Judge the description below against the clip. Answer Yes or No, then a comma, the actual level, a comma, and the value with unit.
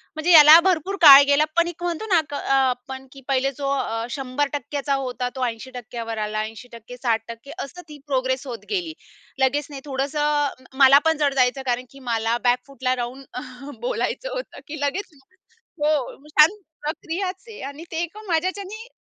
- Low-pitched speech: No, very high, 275 Hz